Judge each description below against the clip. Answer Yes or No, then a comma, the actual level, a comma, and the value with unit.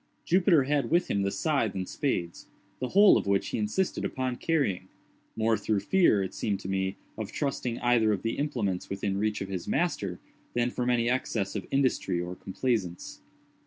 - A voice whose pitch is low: Yes, low, 110 Hz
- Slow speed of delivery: No, average, 175 wpm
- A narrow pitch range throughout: No, wide, 5.4 semitones